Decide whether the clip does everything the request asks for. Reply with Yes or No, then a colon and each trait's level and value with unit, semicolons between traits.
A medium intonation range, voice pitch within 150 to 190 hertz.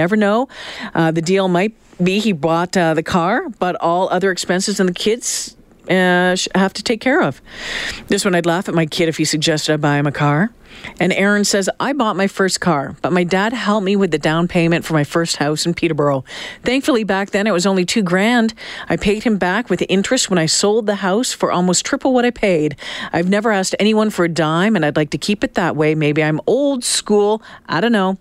Yes: average, 4.1 semitones; medium, 185 Hz